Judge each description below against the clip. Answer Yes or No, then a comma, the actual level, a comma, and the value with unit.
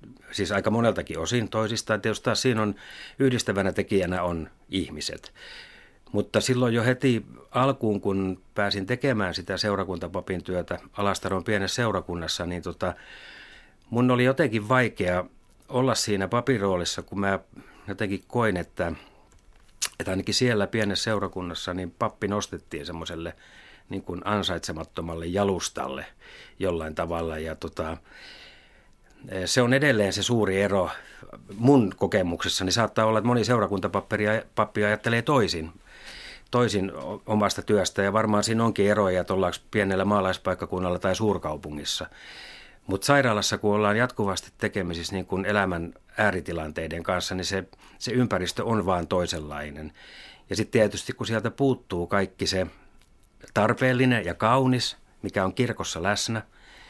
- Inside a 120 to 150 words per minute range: Yes, average, 125 wpm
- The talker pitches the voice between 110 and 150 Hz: No, low, 100 Hz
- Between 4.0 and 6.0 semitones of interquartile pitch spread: No, average, 3.2 semitones